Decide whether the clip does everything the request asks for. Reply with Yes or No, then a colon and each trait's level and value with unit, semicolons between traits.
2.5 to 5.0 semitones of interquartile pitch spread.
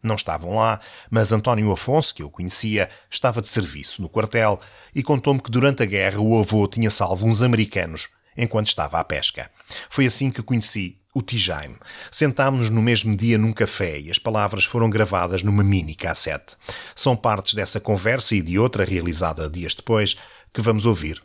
Yes: average, 3.1 semitones